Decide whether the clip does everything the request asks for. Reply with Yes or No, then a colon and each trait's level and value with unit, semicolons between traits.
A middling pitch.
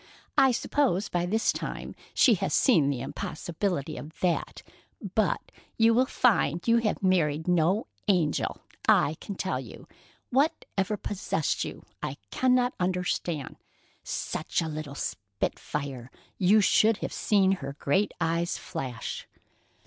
Yes: medium, 180 Hz